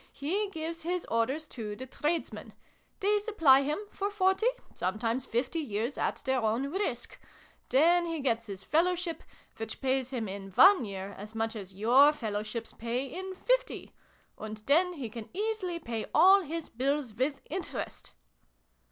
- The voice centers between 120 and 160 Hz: No, very high, 270 Hz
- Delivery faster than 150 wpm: Yes, average, 160 wpm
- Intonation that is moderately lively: No, wide, 7.3 semitones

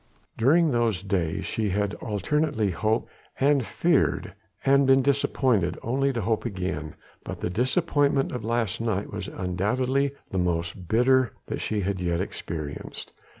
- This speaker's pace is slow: No, average, 145 wpm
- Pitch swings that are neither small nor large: No, wide, 6.0 semitones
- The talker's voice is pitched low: Yes, low, 110 Hz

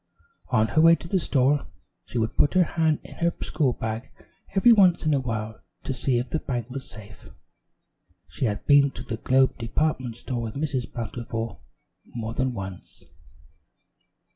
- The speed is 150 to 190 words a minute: Yes, average, 170 wpm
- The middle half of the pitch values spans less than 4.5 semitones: No, average, 5.0 semitones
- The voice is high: No, low, 130 Hz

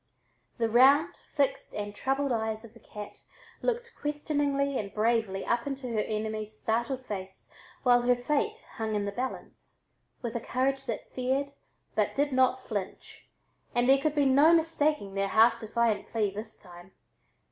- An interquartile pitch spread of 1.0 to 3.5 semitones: No, average, 4.4 semitones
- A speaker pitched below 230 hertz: No, high, 240 Hz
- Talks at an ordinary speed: Yes, average, 160 wpm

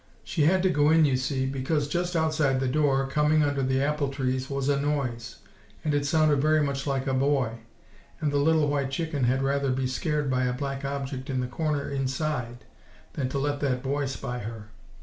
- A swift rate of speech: Yes, fast, 210 wpm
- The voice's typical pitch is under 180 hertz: Yes, medium, 140 Hz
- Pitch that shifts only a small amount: Yes, narrow, 2.1 semitones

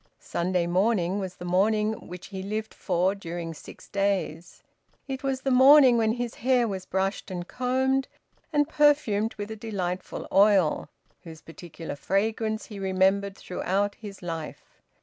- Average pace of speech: Yes, average, 150 wpm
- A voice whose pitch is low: No, high, 200 Hz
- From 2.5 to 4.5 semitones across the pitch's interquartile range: Yes, average, 3.8 semitones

